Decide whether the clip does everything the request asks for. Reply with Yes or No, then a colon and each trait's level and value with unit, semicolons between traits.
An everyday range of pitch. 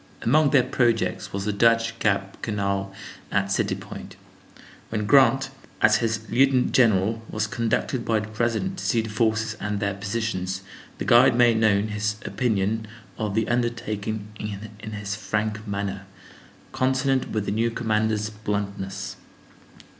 No: narrow, 2.3 semitones